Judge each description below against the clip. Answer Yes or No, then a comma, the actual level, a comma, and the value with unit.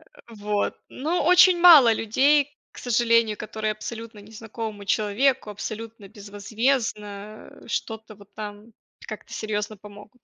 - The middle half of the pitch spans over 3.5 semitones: No, average, 2.8 semitones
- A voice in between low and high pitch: No, high, 220 Hz